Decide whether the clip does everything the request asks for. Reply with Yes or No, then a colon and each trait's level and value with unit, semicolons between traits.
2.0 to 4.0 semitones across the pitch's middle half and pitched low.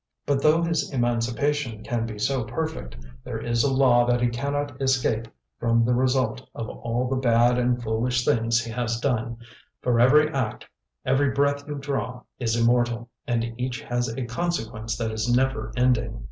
Yes: narrow, 2.5 semitones; low, 120 Hz